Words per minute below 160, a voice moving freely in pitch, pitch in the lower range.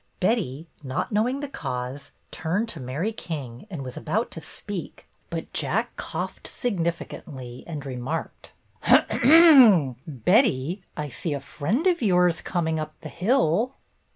No: average, 140 wpm; wide, 7.4 semitones; medium, 165 Hz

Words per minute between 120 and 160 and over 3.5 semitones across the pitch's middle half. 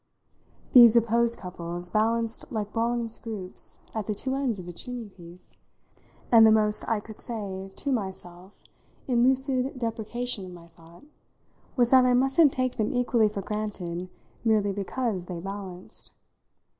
Yes: average, 150 wpm; average, 4.2 semitones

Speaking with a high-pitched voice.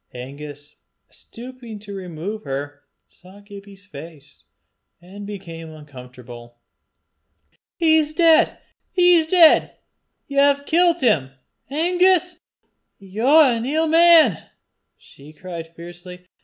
Yes: high, 200 Hz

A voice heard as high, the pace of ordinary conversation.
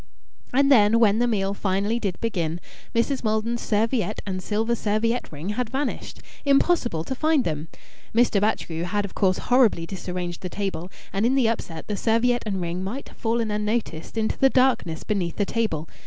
Yes: high, 215 Hz; average, 180 wpm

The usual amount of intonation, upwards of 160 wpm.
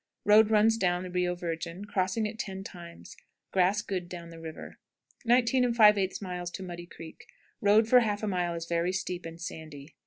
Yes: average, 3.4 semitones; average, 175 wpm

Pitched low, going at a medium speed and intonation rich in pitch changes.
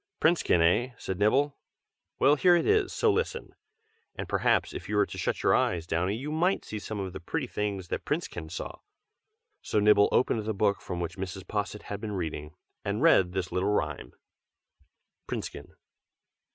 Yes: low, 105 Hz; average, 180 wpm; wide, 6.4 semitones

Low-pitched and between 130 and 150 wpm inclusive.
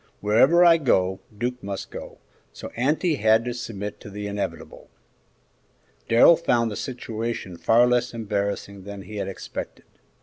Yes: low, 115 Hz; average, 145 wpm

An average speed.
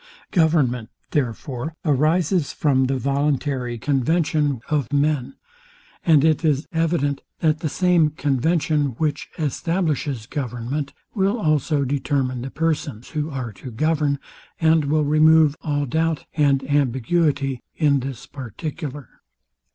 No: slow, 120 wpm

